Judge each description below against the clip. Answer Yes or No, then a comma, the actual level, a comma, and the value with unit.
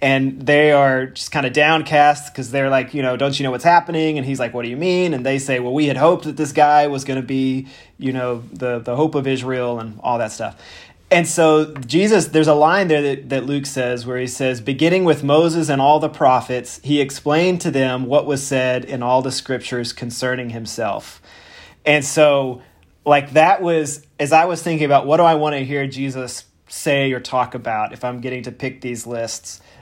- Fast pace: Yes, fast, 225 wpm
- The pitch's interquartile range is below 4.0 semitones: Yes, average, 2.9 semitones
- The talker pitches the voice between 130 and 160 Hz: Yes, low, 135 Hz